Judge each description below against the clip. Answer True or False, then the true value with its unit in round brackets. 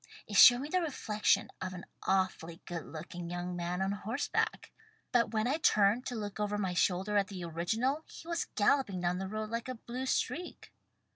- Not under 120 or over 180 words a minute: False (200 wpm)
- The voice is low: False (205 Hz)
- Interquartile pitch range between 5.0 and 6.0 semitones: True (5.3 semitones)